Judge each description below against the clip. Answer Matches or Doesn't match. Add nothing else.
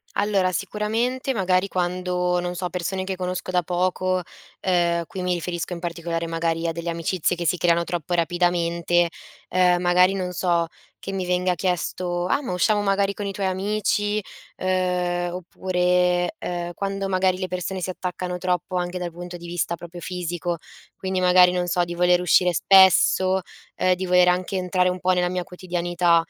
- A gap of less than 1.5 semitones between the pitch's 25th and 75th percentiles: Matches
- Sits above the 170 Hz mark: Matches